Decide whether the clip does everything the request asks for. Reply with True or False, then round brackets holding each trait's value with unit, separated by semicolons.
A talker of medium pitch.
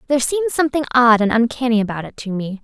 False (225 Hz)